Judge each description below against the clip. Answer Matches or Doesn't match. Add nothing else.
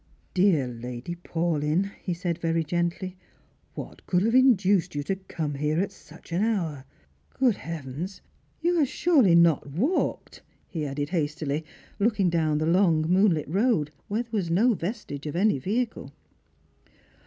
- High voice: Doesn't match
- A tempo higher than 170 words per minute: Doesn't match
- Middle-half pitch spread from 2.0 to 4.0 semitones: Doesn't match